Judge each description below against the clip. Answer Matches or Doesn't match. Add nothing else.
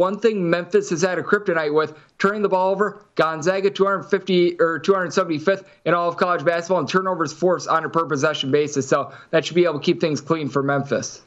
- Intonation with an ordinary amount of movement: Matches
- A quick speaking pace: Matches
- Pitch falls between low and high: Matches